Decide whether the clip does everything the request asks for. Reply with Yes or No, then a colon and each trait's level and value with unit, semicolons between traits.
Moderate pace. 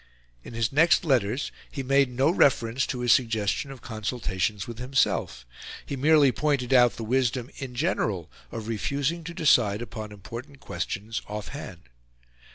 Yes: average, 155 wpm